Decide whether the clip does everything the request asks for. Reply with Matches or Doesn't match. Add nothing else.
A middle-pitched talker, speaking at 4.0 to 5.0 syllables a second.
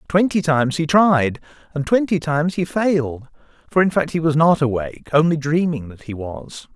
Doesn't match